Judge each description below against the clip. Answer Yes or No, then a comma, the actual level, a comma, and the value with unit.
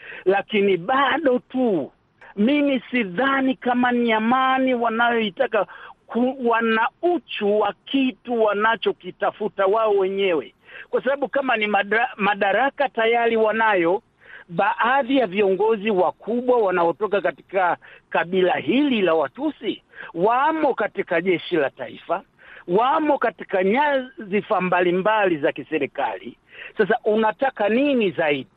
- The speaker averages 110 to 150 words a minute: No, slow, 100 wpm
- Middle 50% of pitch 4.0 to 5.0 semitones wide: Yes, average, 4.5 semitones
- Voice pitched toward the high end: Yes, high, 225 Hz